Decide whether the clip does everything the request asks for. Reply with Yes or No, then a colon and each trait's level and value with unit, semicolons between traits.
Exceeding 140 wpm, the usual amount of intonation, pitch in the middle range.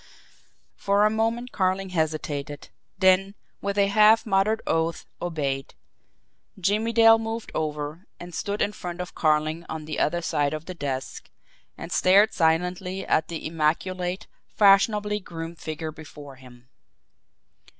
No: slow, 135 wpm; average, 4.4 semitones; medium, 175 Hz